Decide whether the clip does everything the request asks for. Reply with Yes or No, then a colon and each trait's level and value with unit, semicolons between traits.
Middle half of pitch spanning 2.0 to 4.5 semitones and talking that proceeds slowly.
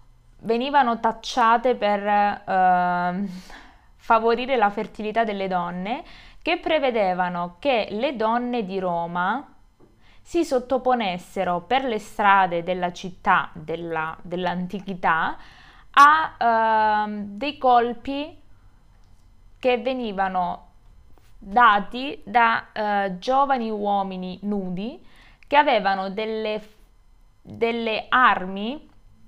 No: average, 4.9 semitones; slow, 85 wpm